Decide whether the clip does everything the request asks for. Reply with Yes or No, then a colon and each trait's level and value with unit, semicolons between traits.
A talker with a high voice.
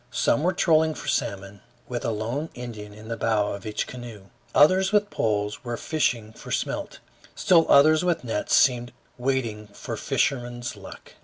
No: low, 120 Hz